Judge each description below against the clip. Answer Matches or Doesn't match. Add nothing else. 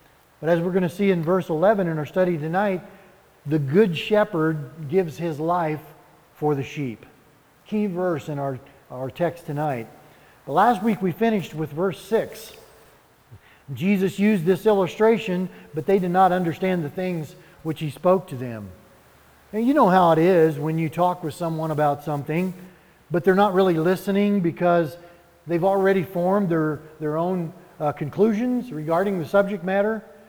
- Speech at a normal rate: Matches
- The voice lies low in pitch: Doesn't match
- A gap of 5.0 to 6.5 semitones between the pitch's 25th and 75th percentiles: Doesn't match